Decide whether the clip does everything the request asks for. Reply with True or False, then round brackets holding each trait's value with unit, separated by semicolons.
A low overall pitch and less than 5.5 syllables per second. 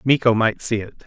True (115 Hz; 5.3 syllables/s)